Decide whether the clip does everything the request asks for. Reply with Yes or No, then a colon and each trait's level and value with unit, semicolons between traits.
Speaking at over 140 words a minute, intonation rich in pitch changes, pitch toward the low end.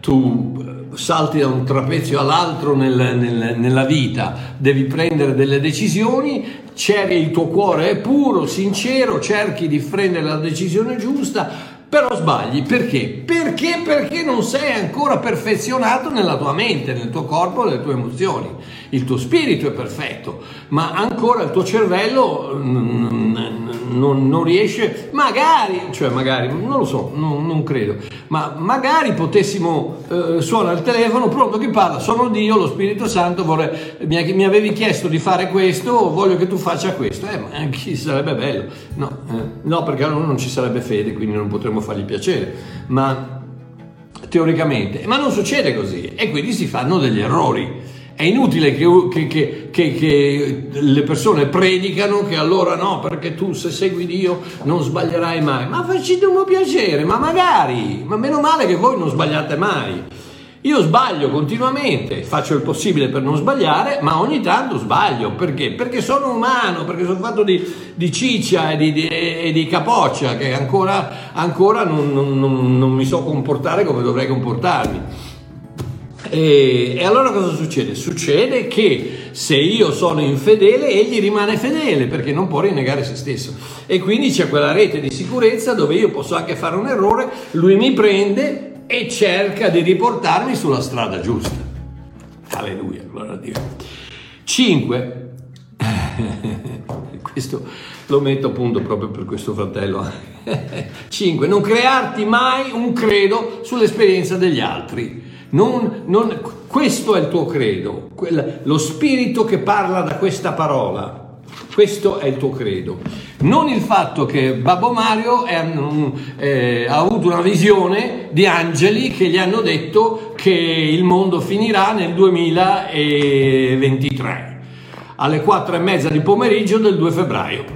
No: average, 150 wpm; wide, 7.2 semitones; medium, 170 Hz